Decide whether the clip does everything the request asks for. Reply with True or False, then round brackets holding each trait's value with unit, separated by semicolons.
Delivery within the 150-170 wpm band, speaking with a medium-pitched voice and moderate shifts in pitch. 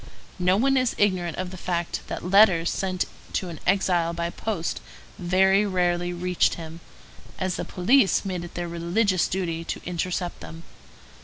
False (160 wpm; 180 Hz; 1.9 semitones)